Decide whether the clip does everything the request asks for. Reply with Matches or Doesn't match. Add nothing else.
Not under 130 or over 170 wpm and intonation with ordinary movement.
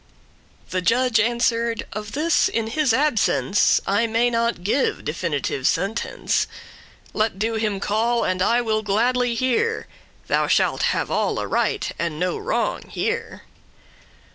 Matches